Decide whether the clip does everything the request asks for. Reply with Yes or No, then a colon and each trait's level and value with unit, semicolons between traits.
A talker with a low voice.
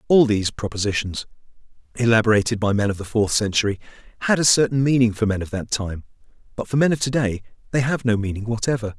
Yes: low, 115 Hz